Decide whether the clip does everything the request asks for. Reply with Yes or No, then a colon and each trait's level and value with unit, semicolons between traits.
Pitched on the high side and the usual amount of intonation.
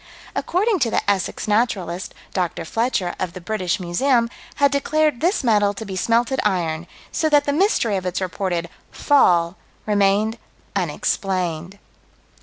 No: high, 205 Hz; wide, 5.7 semitones